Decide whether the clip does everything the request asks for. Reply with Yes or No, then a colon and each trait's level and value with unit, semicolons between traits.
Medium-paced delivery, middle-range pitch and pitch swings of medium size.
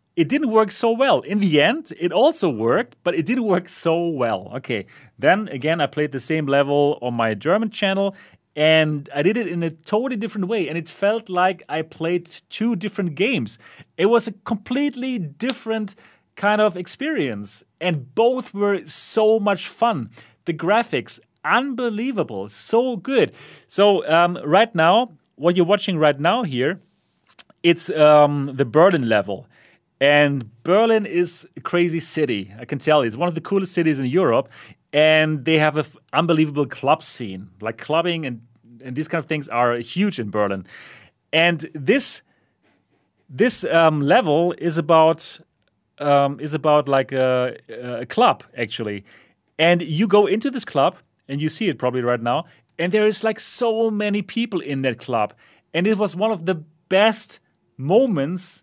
No: average, 170 wpm; medium, 170 Hz; wide, 6.2 semitones